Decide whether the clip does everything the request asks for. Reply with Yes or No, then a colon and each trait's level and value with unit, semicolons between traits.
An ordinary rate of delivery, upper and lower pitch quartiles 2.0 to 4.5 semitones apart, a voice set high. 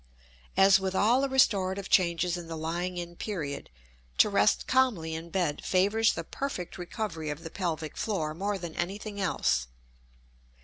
No: average, 160 wpm; average, 3.6 semitones; medium, 180 Hz